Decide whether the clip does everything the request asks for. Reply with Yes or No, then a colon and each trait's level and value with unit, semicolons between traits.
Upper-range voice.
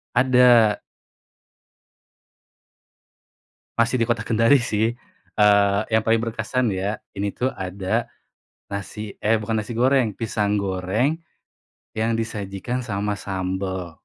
No: low, 110 Hz